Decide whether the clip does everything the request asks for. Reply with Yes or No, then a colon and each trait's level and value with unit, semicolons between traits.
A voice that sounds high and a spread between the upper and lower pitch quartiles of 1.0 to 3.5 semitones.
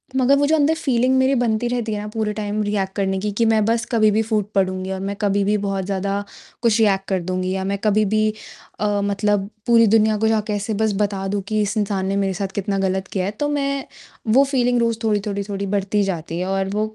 Yes: high, 210 Hz; narrow, 2.4 semitones